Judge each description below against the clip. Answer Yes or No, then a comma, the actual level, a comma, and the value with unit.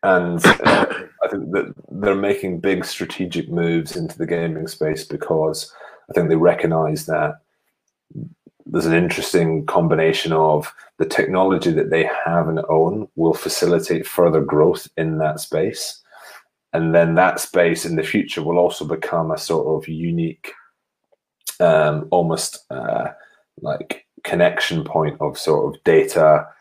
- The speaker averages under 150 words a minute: Yes, average, 140 wpm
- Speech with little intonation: Yes, narrow, 1.7 semitones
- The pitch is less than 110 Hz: Yes, very low, 85 Hz